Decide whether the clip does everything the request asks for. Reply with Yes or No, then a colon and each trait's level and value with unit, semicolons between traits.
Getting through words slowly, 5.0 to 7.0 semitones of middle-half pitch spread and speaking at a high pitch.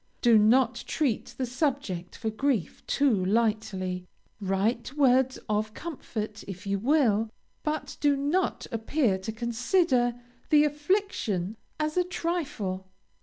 Yes: slow, 125 wpm; wide, 5.6 semitones; high, 235 Hz